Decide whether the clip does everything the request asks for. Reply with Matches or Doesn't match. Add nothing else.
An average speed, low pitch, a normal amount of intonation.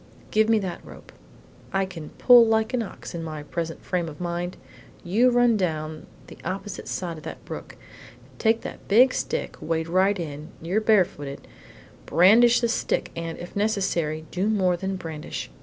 Doesn't match